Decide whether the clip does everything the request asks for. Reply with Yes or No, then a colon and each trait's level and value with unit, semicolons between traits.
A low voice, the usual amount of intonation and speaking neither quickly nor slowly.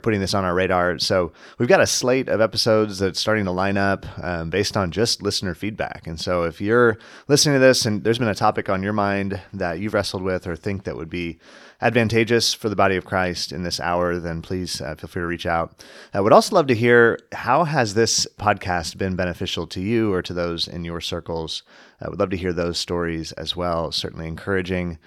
No: very low, 95 Hz; average, 3.7 semitones; fast, 225 wpm